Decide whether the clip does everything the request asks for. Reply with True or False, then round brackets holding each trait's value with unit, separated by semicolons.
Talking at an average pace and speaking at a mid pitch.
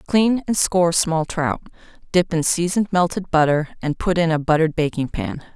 True (185 wpm; 170 Hz)